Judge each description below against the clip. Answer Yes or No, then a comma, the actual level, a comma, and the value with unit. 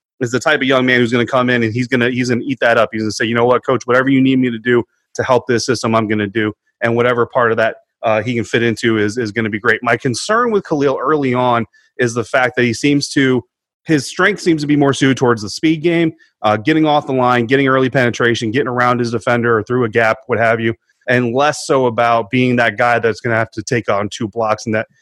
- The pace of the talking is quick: Yes, fast, 290 wpm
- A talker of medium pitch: No, low, 120 Hz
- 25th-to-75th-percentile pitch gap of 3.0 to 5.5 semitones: No, narrow, 2.5 semitones